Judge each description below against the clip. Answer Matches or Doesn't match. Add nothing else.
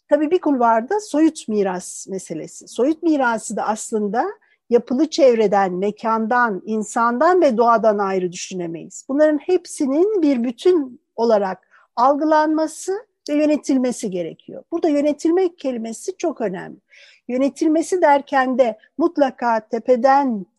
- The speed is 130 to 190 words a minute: Doesn't match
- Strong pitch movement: Matches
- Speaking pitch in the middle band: Doesn't match